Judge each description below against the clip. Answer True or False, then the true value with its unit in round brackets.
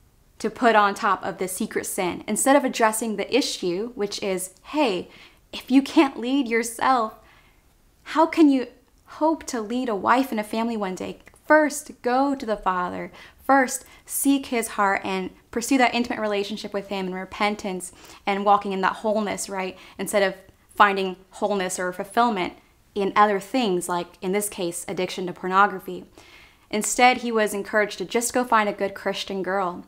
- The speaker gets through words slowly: False (175 wpm)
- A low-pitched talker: False (210 Hz)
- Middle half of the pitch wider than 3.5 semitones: True (4.0 semitones)